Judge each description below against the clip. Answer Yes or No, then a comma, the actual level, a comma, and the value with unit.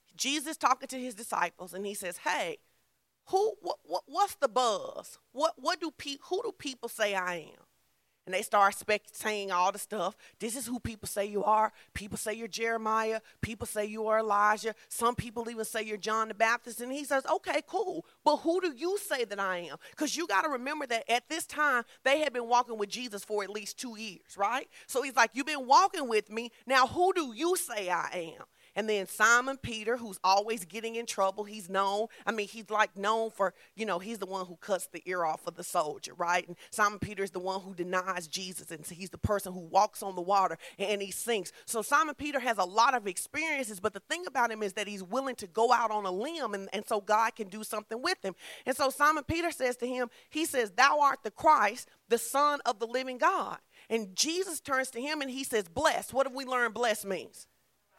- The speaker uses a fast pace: Yes, fast, 230 wpm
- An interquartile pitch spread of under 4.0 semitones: No, average, 5.1 semitones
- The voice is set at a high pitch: Yes, high, 225 Hz